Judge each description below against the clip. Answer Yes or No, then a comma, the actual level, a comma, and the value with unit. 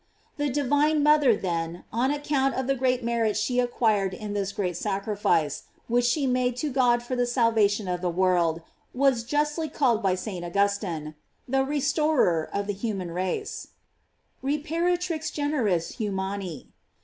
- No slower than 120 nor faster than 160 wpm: Yes, average, 150 wpm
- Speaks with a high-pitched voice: Yes, high, 235 Hz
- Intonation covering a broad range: Yes, wide, 6.1 semitones